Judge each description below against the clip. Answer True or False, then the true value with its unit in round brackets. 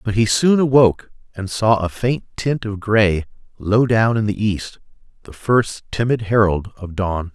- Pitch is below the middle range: True (105 Hz)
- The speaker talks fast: False (180 wpm)